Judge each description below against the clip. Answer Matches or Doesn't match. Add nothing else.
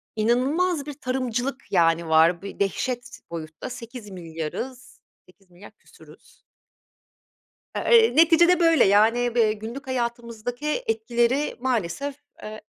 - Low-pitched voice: Doesn't match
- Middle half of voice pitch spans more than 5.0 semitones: Matches